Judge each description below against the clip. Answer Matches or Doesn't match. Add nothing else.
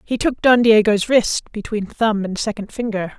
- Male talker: Doesn't match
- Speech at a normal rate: Matches